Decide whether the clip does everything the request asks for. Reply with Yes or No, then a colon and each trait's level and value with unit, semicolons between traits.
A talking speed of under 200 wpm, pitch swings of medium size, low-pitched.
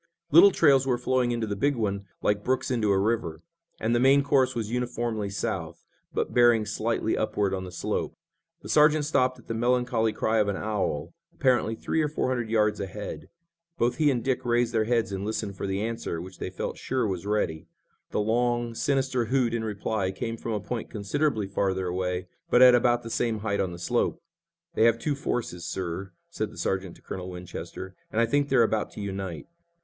No: fast, 205 wpm; average, 3.8 semitones; low, 110 Hz